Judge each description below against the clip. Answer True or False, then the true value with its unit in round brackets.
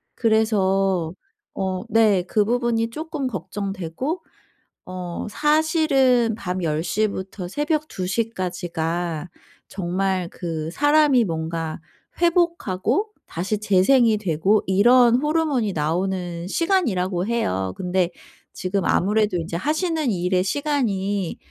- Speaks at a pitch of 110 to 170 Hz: False (200 Hz)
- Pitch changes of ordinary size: False (5.8 semitones)